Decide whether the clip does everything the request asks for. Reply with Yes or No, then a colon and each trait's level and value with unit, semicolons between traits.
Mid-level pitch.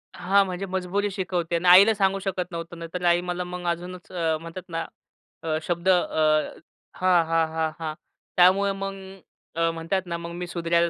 Yes: medium, 175 Hz